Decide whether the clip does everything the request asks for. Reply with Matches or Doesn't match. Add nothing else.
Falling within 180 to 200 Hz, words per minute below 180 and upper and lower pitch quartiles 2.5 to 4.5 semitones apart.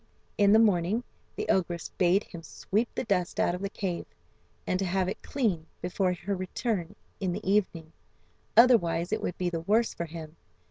Doesn't match